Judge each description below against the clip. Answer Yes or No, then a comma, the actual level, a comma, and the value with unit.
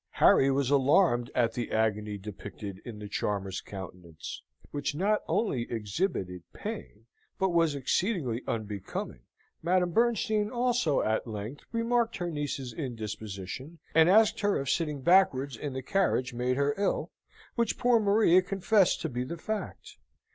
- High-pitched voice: No, medium, 140 Hz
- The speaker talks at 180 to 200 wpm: No, average, 145 wpm